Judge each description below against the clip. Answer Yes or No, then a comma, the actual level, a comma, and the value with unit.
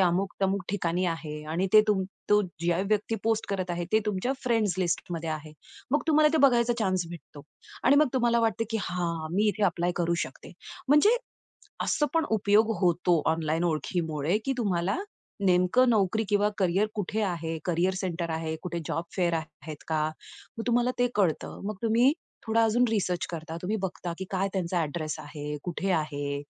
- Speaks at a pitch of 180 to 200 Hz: Yes, medium, 185 Hz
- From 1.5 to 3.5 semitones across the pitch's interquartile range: No, average, 4.6 semitones